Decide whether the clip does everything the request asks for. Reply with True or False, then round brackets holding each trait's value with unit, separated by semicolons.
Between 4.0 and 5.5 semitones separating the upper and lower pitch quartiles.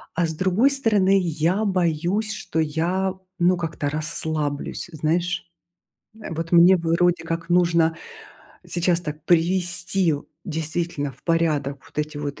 False (2.5 semitones)